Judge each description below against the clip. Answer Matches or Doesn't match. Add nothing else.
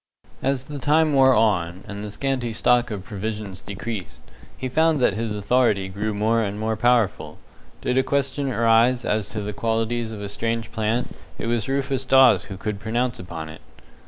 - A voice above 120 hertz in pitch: Doesn't match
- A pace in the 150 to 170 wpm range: Doesn't match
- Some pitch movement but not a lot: Matches